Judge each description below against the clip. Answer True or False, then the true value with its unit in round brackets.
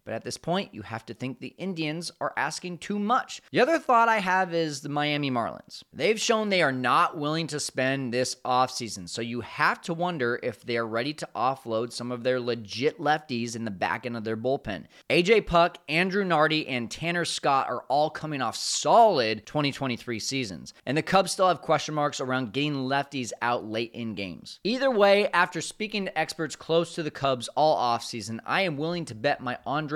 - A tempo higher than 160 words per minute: True (205 wpm)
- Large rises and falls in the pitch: True (6.0 semitones)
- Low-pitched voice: False (145 Hz)